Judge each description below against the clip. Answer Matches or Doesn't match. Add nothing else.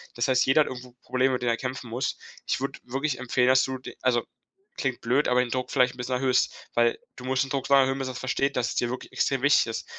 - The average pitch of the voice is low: Matches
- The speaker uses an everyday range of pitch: Doesn't match